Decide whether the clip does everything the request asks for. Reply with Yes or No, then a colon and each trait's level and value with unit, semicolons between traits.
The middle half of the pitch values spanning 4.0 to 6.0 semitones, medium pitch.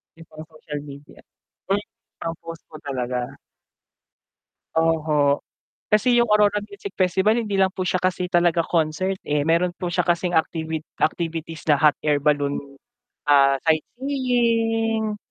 Yes: average, 4.7 semitones; medium, 170 Hz